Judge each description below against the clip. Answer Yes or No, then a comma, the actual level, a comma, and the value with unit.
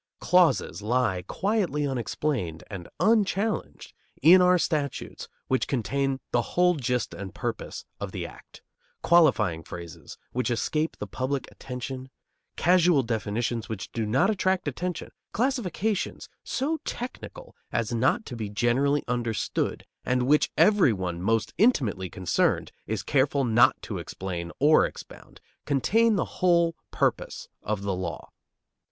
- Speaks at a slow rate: Yes, slow, 130 wpm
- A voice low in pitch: Yes, low, 130 Hz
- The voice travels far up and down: Yes, wide, 8.2 semitones